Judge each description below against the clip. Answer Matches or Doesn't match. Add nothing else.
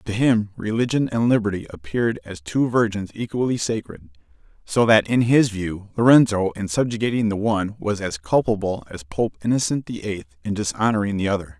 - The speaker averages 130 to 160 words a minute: Doesn't match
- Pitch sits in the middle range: Doesn't match